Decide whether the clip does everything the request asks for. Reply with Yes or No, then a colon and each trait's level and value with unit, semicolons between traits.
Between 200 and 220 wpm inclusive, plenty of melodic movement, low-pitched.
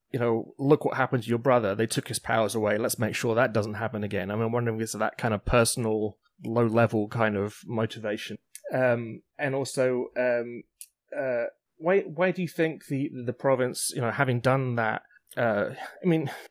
No: fast, 205 wpm; average, 3.3 semitones; low, 120 Hz